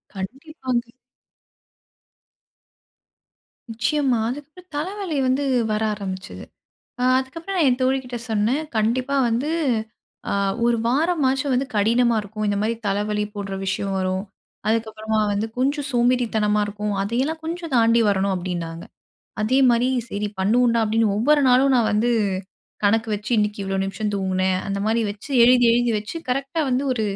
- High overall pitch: Yes, high, 230 Hz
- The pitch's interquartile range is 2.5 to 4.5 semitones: Yes, average, 4.1 semitones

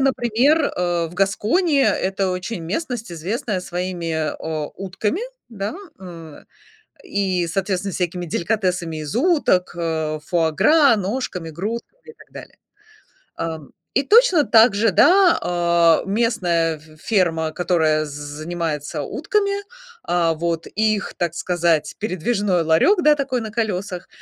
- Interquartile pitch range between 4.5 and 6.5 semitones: Yes, wide, 5.4 semitones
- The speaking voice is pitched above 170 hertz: Yes, medium, 185 Hz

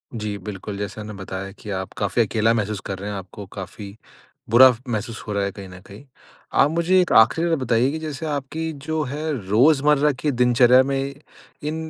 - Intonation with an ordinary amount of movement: No, wide, 6.1 semitones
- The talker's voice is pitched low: Yes, low, 115 Hz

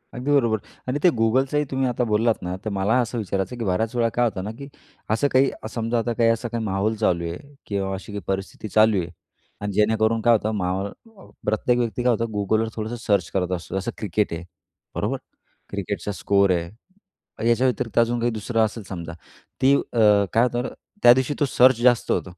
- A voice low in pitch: Yes, low, 110 Hz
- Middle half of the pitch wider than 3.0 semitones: Yes, average, 3.4 semitones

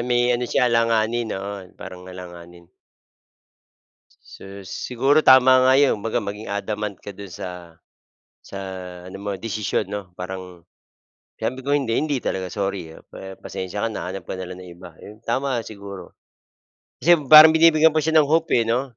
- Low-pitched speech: Yes, low, 105 Hz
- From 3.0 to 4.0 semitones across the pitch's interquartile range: No, wide, 5.4 semitones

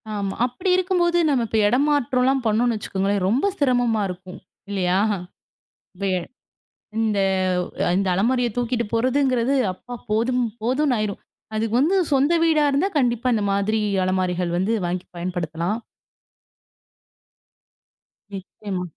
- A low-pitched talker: No, high, 225 Hz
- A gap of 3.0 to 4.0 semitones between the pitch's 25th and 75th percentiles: No, average, 4.8 semitones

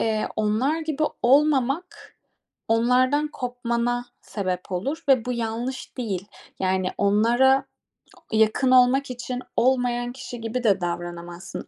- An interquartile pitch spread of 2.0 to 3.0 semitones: No, average, 3.5 semitones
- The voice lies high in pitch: Yes, high, 245 Hz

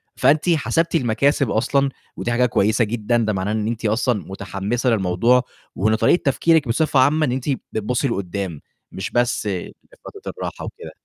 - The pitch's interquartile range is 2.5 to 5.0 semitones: Yes, average, 4.6 semitones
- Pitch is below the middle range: Yes, low, 120 Hz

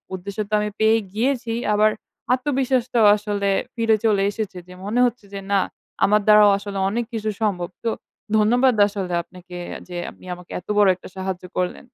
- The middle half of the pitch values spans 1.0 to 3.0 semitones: Yes, average, 2.7 semitones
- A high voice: Yes, high, 210 Hz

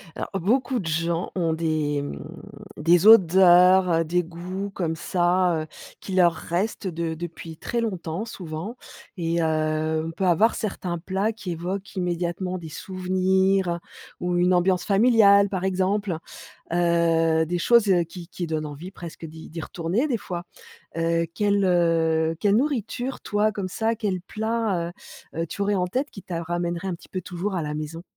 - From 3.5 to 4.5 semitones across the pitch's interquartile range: No, average, 2.9 semitones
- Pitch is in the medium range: Yes, medium, 180 Hz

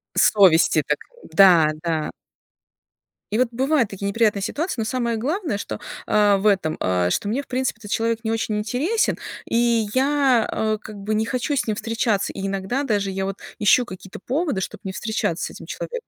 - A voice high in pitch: Yes, high, 215 Hz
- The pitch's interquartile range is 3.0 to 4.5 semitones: Yes, average, 4.2 semitones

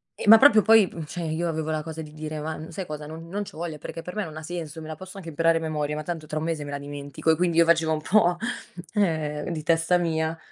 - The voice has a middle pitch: Yes, medium, 160 Hz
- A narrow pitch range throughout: Yes, narrow, 2.0 semitones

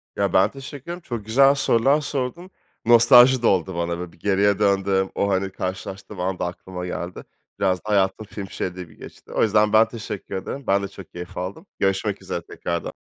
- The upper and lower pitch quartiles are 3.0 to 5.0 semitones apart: Yes, average, 3.9 semitones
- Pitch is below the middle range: Yes, low, 100 Hz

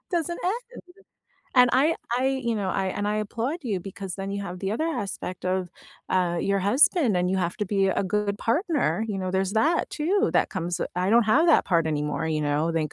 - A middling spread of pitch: No, wide, 5.7 semitones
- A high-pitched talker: Yes, high, 200 Hz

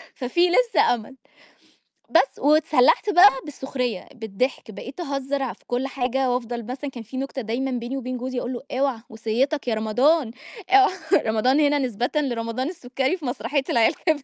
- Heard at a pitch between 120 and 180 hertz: No, very high, 260 Hz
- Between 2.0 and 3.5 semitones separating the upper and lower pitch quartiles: Yes, average, 3.0 semitones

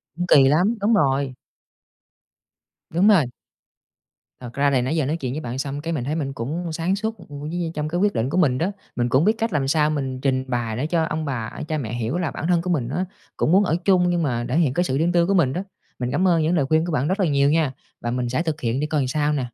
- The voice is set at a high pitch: No, medium, 150 Hz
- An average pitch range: Yes, average, 4.7 semitones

